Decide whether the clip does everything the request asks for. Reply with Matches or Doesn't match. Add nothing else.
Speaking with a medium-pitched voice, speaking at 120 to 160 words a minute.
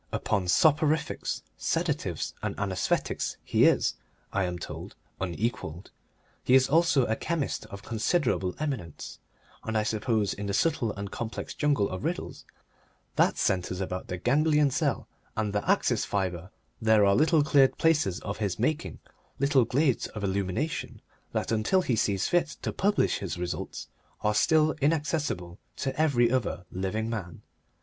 Doesn't match